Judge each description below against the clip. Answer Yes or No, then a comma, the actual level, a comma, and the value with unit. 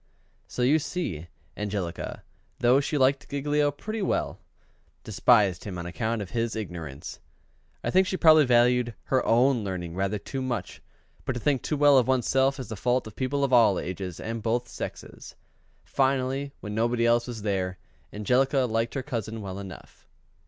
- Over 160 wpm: Yes, average, 175 wpm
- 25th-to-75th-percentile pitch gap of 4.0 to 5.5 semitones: Yes, average, 4.6 semitones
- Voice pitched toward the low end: Yes, low, 120 Hz